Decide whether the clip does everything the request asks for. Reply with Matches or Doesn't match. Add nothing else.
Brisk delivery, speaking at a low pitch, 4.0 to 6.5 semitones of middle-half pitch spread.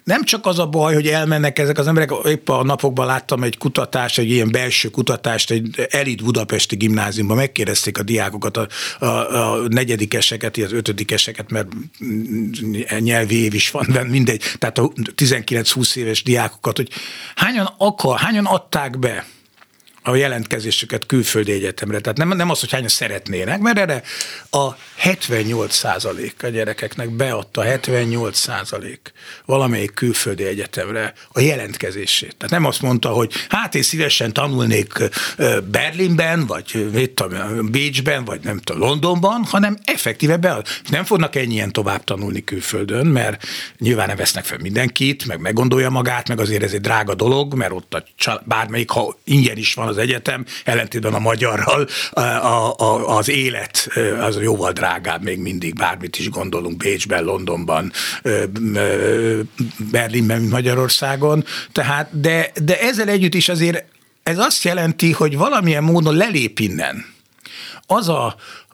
Doesn't match